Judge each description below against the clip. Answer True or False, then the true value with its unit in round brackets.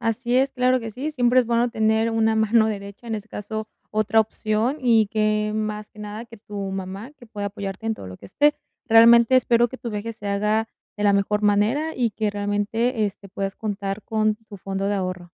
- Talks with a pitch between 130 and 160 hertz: False (215 Hz)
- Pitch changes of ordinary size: False (2.2 semitones)